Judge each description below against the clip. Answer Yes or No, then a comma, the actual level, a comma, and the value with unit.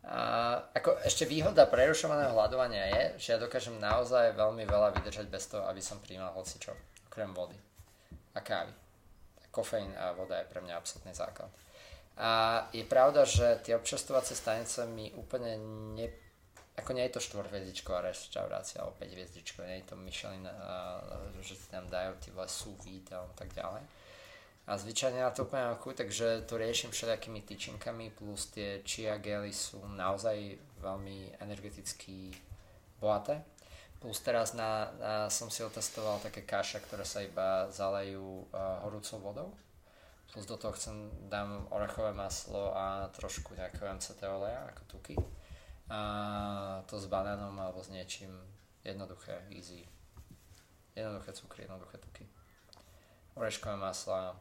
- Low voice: Yes, low, 100 Hz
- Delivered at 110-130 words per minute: No, average, 145 wpm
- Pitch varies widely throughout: No, average, 2.7 semitones